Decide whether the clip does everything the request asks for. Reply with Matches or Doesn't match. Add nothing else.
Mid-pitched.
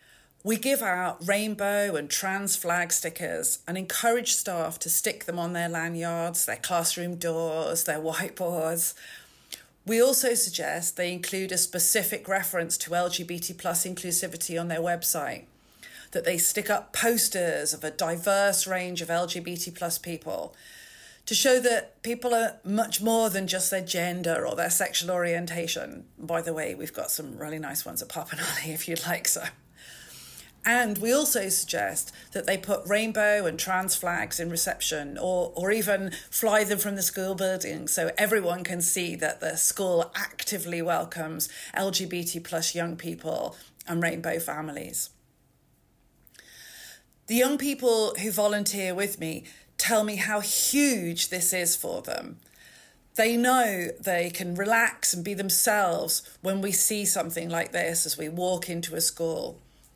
Matches